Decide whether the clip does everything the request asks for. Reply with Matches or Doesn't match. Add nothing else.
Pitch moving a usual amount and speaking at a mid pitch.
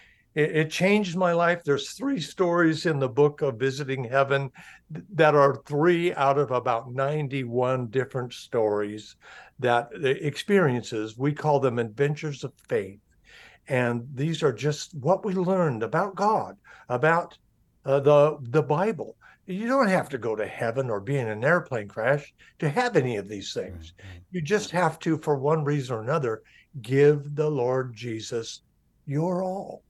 Matches